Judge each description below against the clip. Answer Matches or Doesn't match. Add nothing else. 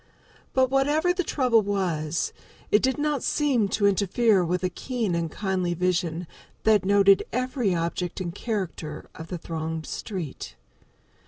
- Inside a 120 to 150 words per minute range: Matches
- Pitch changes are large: Matches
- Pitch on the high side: Matches